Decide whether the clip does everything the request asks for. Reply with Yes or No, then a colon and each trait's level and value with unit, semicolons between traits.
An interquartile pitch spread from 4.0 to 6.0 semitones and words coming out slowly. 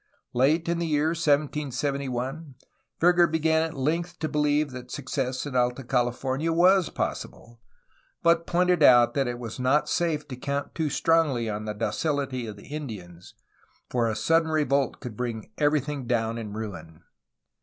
No: average, 4.6 semitones; average, 160 wpm